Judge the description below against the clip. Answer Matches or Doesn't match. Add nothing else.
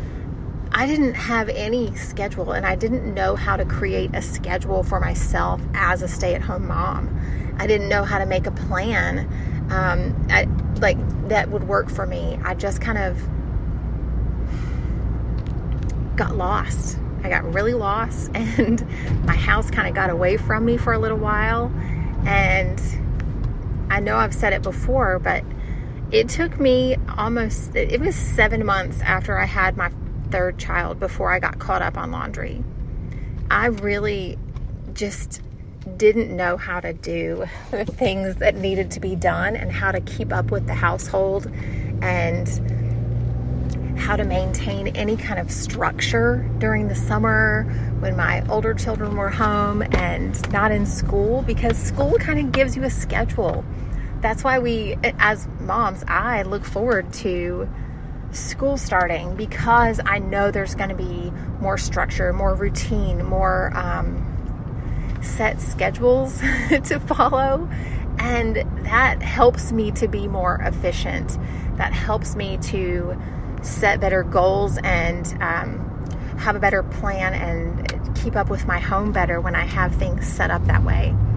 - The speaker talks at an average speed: Matches